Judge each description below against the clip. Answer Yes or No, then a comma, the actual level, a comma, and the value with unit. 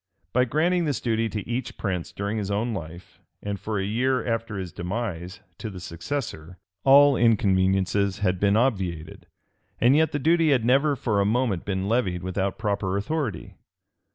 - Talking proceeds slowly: No, average, 170 wpm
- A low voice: Yes, low, 105 Hz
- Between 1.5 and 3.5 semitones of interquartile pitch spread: No, average, 5.0 semitones